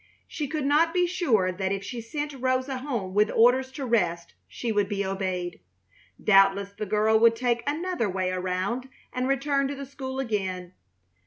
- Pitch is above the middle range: Yes, high, 230 Hz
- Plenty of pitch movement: Yes, wide, 5.7 semitones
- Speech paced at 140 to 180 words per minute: Yes, average, 175 wpm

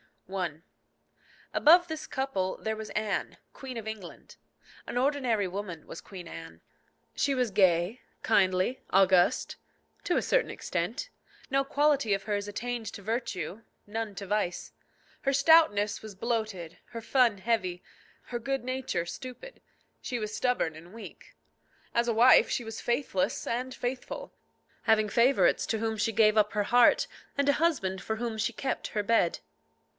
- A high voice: Yes, high, 220 Hz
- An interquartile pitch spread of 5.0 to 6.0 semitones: No, average, 4.4 semitones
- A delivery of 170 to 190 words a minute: No, average, 155 wpm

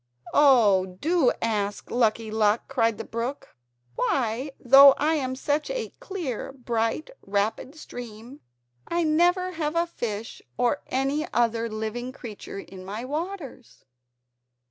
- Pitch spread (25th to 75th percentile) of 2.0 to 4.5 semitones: No, average, 5.2 semitones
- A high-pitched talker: Yes, very high, 250 Hz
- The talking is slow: Yes, slow, 125 wpm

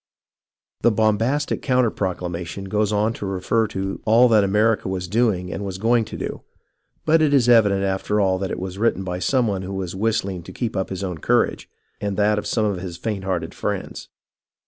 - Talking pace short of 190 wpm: No, fast, 205 wpm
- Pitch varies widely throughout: No, average, 3.1 semitones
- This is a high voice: No, low, 100 Hz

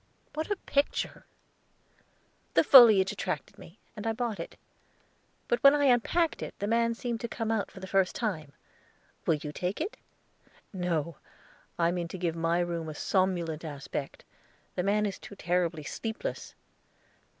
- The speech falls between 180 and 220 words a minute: No, average, 160 wpm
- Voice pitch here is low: No, high, 190 Hz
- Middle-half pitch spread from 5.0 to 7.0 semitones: Yes, wide, 5.4 semitones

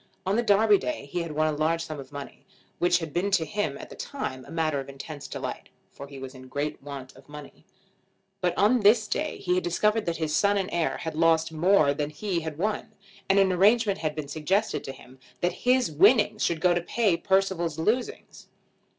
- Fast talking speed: Yes, fast, 220 wpm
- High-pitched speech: No, medium, 170 Hz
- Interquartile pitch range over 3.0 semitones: Yes, average, 5.2 semitones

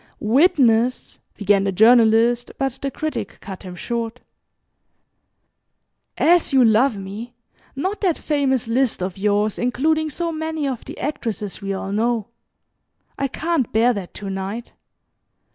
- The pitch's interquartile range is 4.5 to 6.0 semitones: Yes, average, 5.0 semitones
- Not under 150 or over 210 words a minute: No, average, 140 wpm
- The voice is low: No, high, 240 Hz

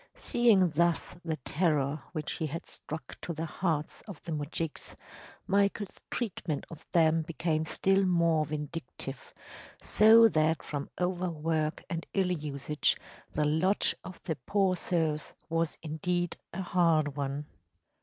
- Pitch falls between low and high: Yes, medium, 165 Hz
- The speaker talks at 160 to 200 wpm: No, slow, 135 wpm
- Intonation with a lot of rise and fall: No, average, 2.8 semitones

